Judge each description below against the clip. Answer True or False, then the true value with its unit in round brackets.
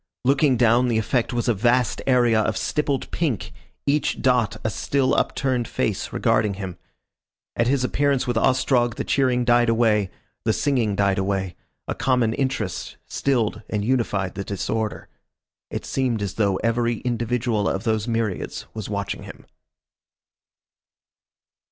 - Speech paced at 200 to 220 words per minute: False (145 wpm)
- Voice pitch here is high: False (120 Hz)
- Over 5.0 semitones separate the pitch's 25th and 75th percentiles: False (3.1 semitones)